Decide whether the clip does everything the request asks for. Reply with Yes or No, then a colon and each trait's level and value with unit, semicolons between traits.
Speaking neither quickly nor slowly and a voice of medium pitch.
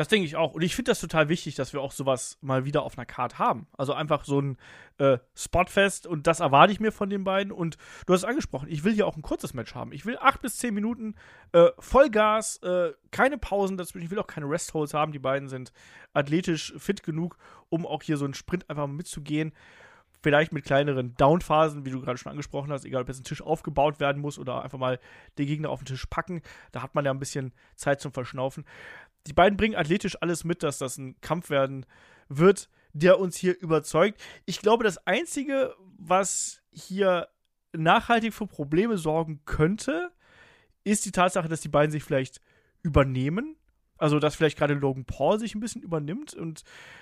No: fast, 205 wpm; medium, 160 Hz